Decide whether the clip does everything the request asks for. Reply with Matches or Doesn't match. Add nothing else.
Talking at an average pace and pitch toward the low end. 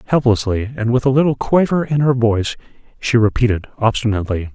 Matches